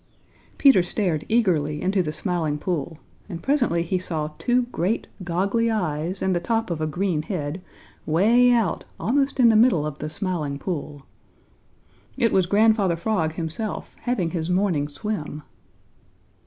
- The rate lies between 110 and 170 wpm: Yes, average, 150 wpm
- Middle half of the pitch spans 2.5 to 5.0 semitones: No, wide, 5.6 semitones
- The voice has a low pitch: No, medium, 180 Hz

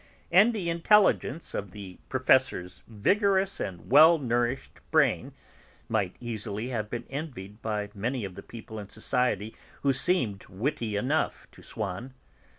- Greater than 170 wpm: No, average, 140 wpm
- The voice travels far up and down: Yes, wide, 5.8 semitones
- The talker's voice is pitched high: No, low, 120 Hz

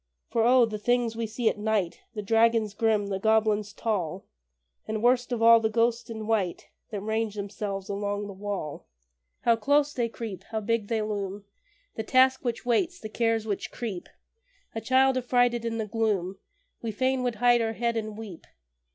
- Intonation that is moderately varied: No, narrow, 2.3 semitones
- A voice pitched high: Yes, high, 225 Hz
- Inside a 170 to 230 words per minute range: Yes, average, 185 wpm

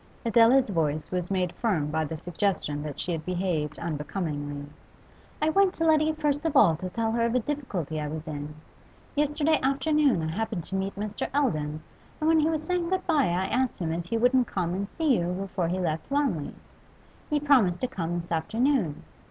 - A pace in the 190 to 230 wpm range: Yes, average, 200 wpm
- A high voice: Yes, high, 195 Hz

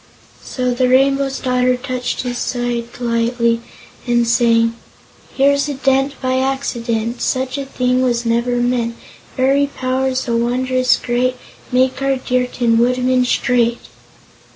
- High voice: Yes, very high, 250 Hz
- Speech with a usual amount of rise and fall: No, narrow, 1.5 semitones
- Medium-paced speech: No, slow, 130 wpm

